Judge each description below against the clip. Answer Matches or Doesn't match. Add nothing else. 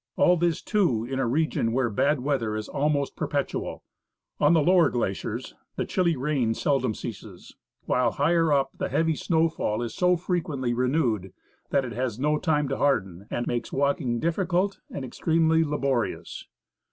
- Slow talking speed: Doesn't match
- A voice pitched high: Doesn't match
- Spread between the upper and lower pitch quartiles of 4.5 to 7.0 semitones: Matches